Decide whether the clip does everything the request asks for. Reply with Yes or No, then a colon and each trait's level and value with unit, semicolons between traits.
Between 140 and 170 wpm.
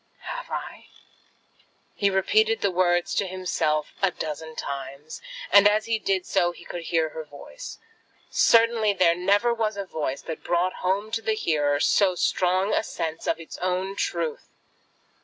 Yes: average, 160 wpm